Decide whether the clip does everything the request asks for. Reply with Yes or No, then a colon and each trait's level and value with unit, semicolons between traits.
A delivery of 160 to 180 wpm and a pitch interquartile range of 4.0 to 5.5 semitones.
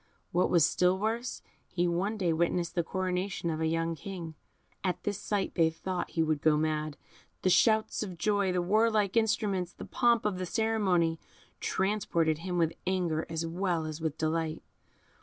No: average, 170 wpm; average, 3.5 semitones